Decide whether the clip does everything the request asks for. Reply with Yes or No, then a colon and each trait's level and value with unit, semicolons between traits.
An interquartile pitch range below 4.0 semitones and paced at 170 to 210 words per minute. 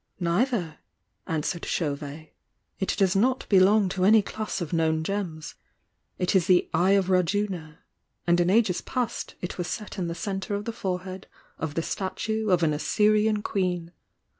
Yes: average, 3.5 semitones; average, 175 wpm